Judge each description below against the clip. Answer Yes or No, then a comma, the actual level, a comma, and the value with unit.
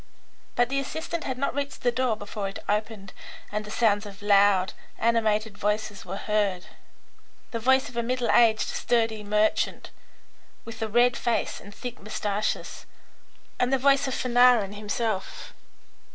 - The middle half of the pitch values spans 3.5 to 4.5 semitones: No, average, 3.0 semitones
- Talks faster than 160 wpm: No, average, 150 wpm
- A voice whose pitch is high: Yes, high, 220 Hz